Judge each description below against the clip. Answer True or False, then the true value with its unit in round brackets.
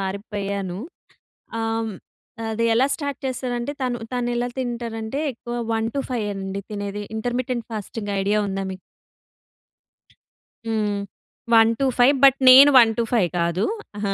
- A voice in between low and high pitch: False (225 Hz)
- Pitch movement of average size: True (3.2 semitones)